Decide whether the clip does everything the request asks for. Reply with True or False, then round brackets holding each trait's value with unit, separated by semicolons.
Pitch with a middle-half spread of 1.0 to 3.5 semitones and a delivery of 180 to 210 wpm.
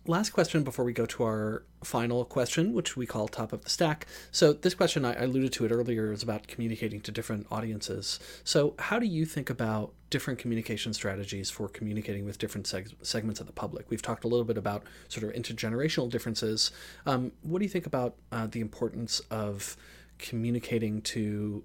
True (2.7 semitones; 190 wpm)